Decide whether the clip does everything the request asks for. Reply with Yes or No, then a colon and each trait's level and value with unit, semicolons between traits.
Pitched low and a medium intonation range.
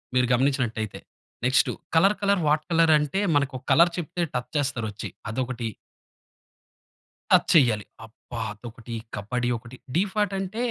No: low, 130 Hz; wide, 6.1 semitones